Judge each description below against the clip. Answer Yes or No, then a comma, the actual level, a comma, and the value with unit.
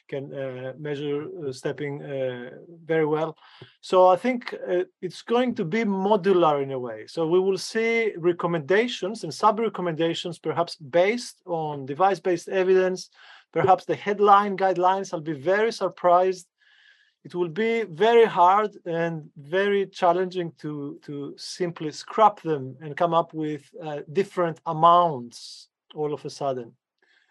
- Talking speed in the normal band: Yes, average, 145 wpm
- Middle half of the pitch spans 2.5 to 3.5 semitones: No, average, 4.2 semitones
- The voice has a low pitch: No, medium, 175 Hz